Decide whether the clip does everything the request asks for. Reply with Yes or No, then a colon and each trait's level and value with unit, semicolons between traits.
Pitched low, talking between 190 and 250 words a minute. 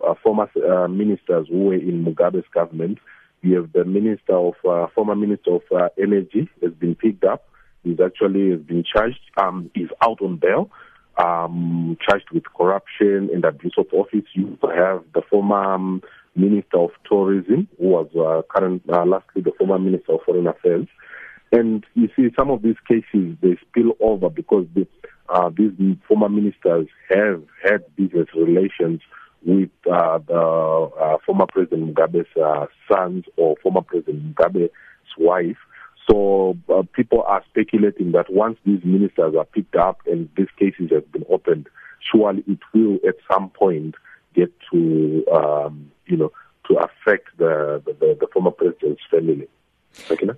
No: very low, 95 Hz; average, 160 wpm